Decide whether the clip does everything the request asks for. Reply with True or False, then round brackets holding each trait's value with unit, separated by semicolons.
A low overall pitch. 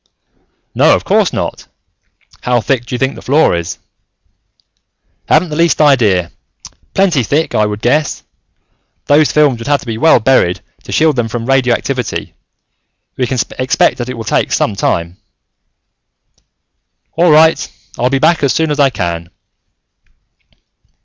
True (130 Hz)